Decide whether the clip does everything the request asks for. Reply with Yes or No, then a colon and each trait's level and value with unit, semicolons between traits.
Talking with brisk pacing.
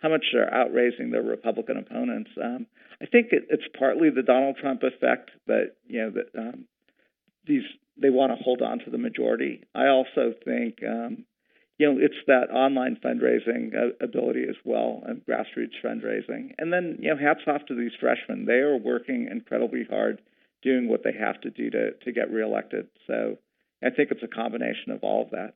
No: average, 190 wpm